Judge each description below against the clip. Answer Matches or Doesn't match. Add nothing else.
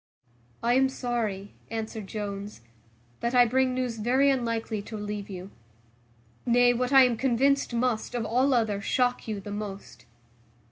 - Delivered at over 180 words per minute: Doesn't match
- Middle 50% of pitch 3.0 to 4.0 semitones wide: Matches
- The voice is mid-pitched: Doesn't match